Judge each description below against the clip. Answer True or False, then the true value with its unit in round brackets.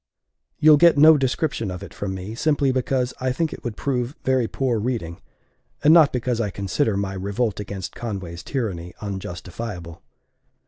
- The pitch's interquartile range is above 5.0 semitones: True (5.5 semitones)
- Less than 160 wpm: False (165 wpm)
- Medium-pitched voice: False (115 Hz)